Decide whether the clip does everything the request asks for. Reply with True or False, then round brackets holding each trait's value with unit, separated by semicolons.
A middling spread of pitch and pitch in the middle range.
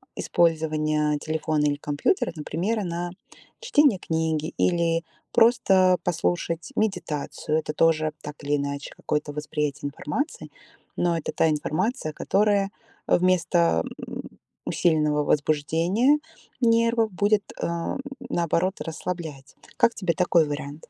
True (3.8 semitones; 165 Hz)